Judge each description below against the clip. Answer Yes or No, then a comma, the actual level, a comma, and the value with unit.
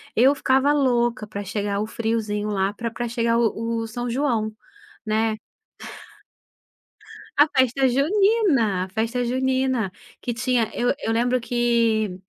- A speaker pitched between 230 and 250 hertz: Yes, high, 235 Hz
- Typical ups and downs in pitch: Yes, average, 3.0 semitones